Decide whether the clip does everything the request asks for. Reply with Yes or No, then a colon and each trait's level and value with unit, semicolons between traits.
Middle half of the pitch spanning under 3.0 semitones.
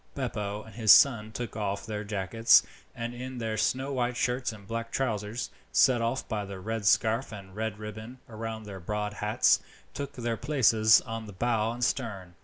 Yes: narrow, 2.5 semitones